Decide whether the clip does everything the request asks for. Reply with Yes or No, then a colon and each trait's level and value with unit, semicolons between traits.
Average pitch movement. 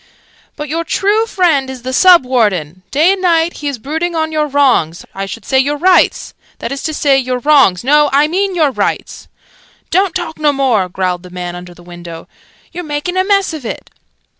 No: wide, 7.6 semitones